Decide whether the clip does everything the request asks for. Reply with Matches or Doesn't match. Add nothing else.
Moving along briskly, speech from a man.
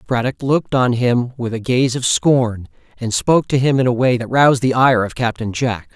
Matches